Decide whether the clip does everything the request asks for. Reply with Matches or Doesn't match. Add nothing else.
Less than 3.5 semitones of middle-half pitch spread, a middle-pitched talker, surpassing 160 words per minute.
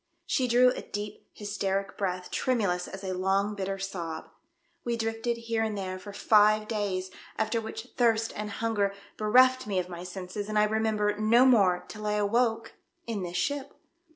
Doesn't match